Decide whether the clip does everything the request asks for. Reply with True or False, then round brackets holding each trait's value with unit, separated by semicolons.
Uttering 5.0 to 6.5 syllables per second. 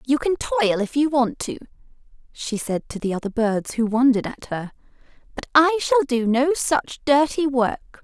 False (4.5 syllables/s)